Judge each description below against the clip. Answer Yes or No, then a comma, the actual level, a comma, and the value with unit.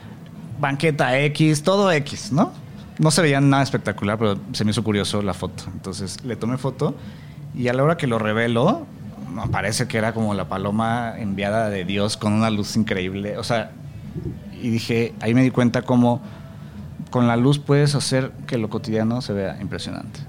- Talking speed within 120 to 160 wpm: No, average, 185 wpm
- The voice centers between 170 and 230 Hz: No, low, 115 Hz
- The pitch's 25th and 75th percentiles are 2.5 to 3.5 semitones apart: No, average, 4.3 semitones